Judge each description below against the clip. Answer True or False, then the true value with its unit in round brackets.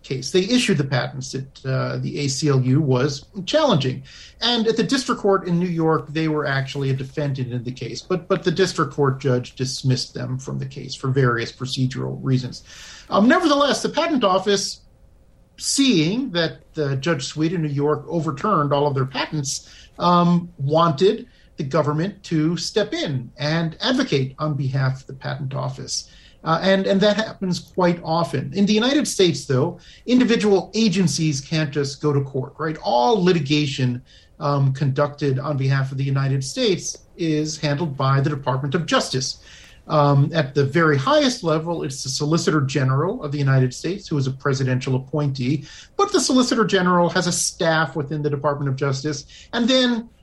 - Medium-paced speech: True (175 wpm)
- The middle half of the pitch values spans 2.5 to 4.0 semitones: False (4.8 semitones)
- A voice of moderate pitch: True (150 Hz)